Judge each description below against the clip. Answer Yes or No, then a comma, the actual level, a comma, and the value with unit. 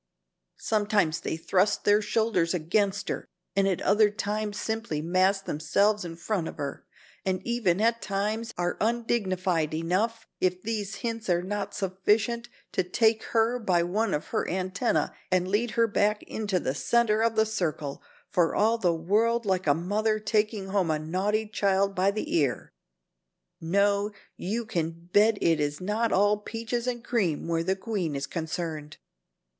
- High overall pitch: Yes, high, 200 Hz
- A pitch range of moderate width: Yes, average, 3.8 semitones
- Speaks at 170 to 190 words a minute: No, average, 160 wpm